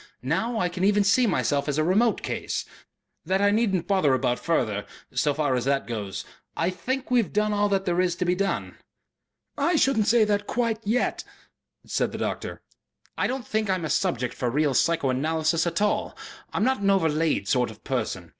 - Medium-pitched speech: Yes, medium, 180 Hz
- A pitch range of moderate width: No, wide, 6.1 semitones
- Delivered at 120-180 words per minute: No, average, 195 wpm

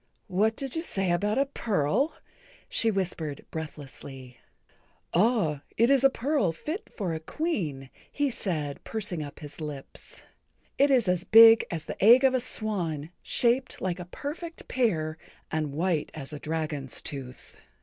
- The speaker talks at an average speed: Yes, average, 150 wpm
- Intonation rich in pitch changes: Yes, wide, 7.8 semitones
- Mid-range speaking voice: Yes, medium, 180 Hz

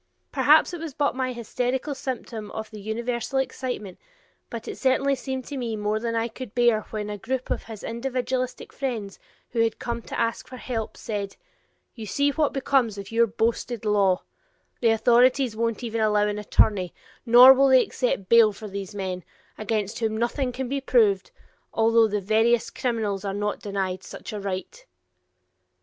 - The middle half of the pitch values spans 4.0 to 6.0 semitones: No, average, 3.3 semitones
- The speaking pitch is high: Yes, high, 230 Hz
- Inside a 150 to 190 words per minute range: Yes, average, 175 wpm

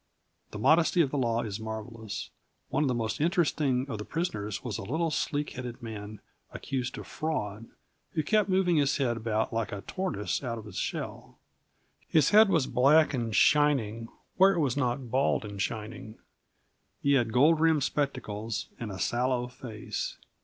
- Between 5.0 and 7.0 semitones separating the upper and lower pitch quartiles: Yes, average, 5.3 semitones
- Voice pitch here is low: Yes, low, 125 Hz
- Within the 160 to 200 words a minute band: Yes, average, 175 wpm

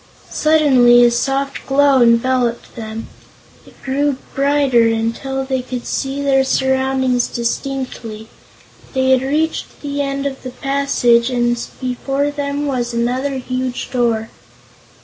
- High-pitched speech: Yes, very high, 260 Hz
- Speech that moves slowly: Yes, slow, 125 wpm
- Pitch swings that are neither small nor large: No, narrow, 2.3 semitones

